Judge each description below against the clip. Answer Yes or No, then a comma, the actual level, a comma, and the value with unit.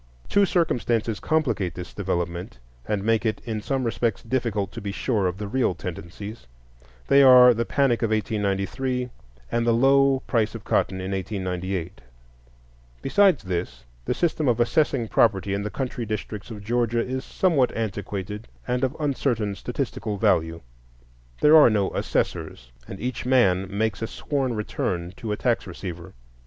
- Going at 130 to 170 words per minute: Yes, average, 155 wpm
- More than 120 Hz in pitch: No, low, 110 Hz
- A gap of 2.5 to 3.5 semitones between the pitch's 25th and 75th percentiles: No, average, 4.4 semitones